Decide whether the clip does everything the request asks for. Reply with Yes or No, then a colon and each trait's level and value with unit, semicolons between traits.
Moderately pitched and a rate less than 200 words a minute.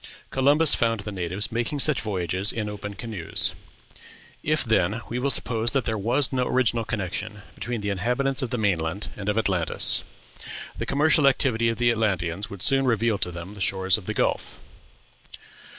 No: low, 110 Hz; average, 180 wpm